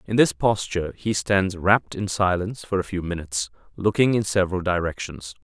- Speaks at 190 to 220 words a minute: No, average, 175 wpm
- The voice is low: Yes, very low, 95 Hz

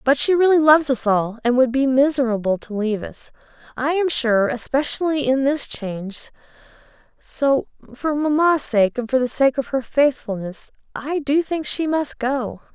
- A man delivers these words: No, female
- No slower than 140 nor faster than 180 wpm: Yes, average, 170 wpm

